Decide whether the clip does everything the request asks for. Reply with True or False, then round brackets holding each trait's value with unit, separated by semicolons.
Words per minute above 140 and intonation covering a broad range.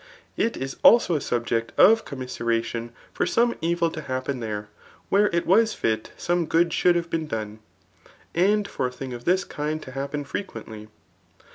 True (170 wpm; 6.6 semitones)